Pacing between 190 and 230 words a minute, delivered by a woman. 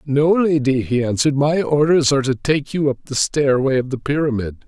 No: fast, 205 wpm; male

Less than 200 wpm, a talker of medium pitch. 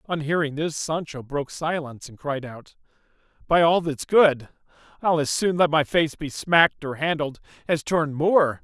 Yes: average, 180 wpm; medium, 150 Hz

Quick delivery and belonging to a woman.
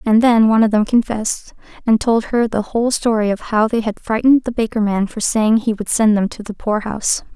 Yes: fast, 245 wpm; female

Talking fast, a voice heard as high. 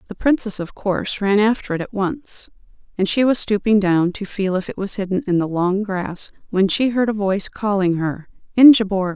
Yes: fast, 210 wpm; high, 200 Hz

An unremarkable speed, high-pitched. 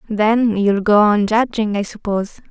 Yes: average, 170 wpm; high, 210 Hz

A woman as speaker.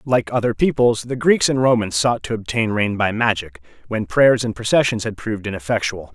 No: male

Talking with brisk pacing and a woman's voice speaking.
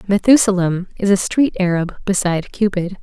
No: average, 140 wpm; female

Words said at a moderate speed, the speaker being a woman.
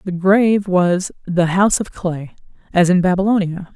Yes: average, 160 wpm; female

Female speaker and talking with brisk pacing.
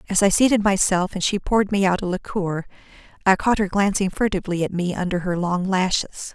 Yes: female; fast, 210 wpm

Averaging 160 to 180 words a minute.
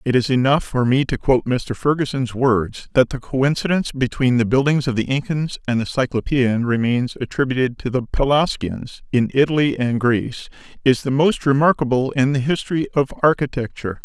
Yes: average, 170 wpm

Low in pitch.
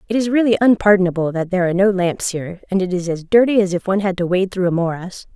No: high, 190 Hz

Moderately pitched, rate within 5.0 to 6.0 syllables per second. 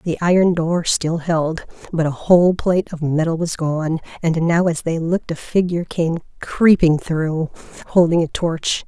No: medium, 165 Hz; 4.6 syllables/s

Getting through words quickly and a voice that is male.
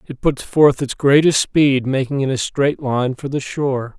Yes: fast, 210 wpm; male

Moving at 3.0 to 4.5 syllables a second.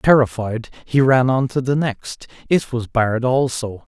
Yes: 4.3 syllables/s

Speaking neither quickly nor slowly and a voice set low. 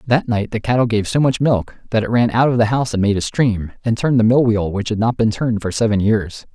No: fast, 295 wpm; low, 115 Hz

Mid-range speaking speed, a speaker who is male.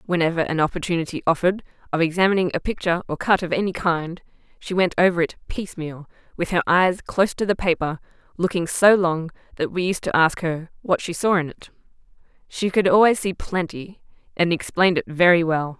No: average, 185 wpm; female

